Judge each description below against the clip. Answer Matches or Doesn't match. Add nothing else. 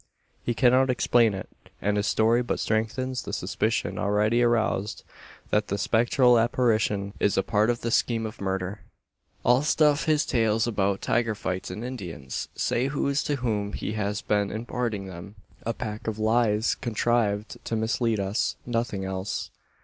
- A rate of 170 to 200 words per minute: Doesn't match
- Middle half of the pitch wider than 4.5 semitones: Doesn't match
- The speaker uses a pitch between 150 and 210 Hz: Doesn't match